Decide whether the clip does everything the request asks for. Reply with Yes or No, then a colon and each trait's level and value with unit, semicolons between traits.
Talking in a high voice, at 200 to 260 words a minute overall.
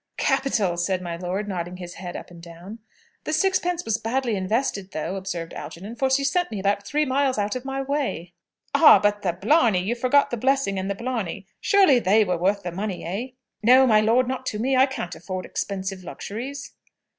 Yes: high, 210 Hz; fast, 205 wpm